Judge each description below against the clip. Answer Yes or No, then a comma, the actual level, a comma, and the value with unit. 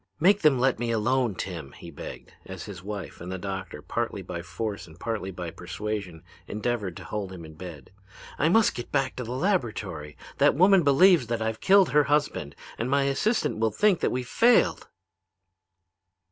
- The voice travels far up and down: Yes, wide, 7.1 semitones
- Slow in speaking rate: No, average, 185 wpm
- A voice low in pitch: Yes, low, 110 Hz